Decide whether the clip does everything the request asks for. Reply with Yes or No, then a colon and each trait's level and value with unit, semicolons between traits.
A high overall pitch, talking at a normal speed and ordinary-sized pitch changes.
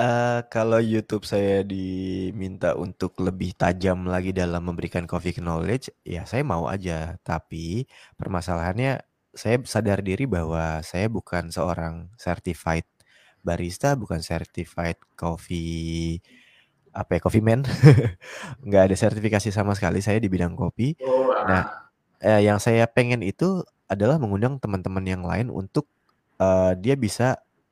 No: very low, 95 Hz; average, 130 wpm; average, 4.2 semitones